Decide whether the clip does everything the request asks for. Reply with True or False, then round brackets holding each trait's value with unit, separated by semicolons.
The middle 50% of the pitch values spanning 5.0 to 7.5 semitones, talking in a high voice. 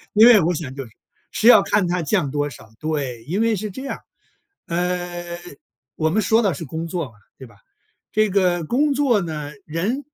False (5.6 semitones; 175 Hz)